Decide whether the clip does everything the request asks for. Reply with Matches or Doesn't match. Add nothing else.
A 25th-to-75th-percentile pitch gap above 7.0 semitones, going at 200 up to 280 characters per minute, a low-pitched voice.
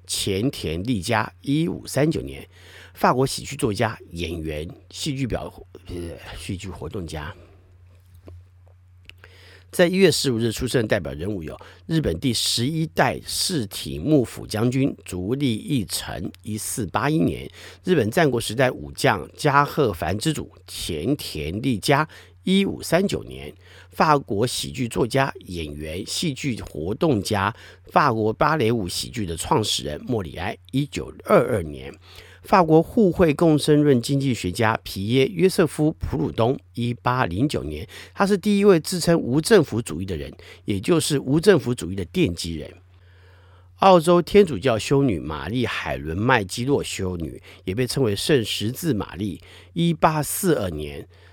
Matches